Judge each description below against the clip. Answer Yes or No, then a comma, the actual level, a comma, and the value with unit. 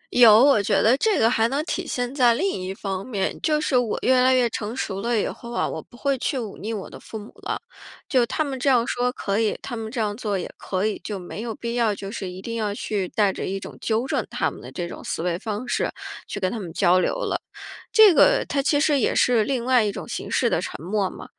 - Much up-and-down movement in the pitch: No, average, 4.0 semitones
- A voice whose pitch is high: Yes, high, 230 Hz